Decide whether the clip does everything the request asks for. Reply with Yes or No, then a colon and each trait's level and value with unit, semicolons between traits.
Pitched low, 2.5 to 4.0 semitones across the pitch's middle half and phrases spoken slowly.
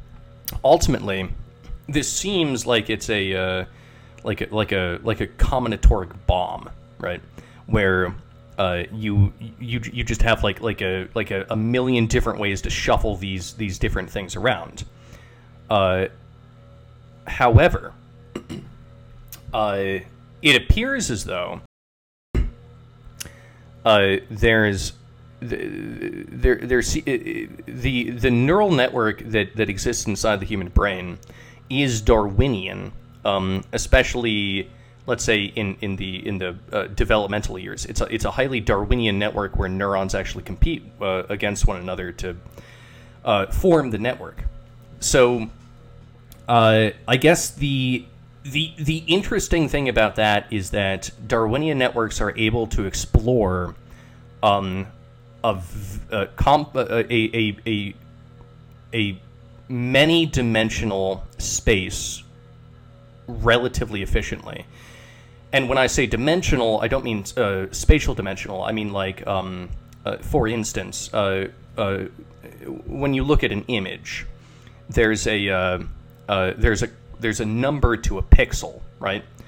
Yes: low, 115 Hz; average, 3.7 semitones; slow, 125 wpm